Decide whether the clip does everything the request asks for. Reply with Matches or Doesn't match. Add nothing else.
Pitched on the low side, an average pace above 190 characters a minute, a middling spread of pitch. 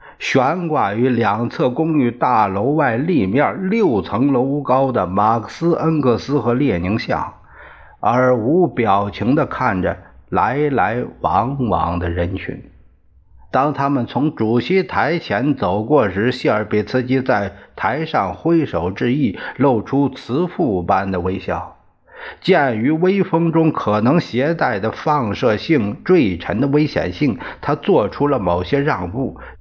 Doesn't match